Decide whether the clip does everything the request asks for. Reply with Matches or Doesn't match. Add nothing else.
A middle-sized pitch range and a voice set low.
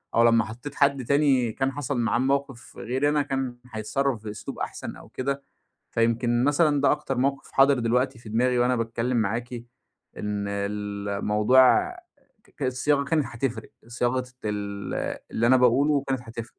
Matches